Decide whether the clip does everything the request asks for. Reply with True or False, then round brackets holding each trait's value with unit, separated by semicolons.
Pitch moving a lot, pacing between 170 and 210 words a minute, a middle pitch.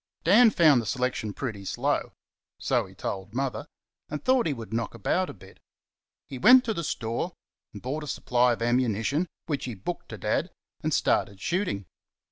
False (6.7 semitones; 180 wpm; 130 Hz)